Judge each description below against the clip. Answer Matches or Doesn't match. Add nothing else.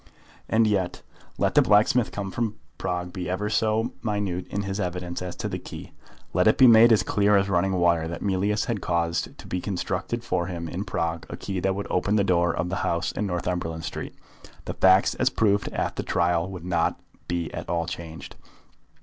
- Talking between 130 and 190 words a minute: Doesn't match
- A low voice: Matches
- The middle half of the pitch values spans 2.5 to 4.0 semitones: Matches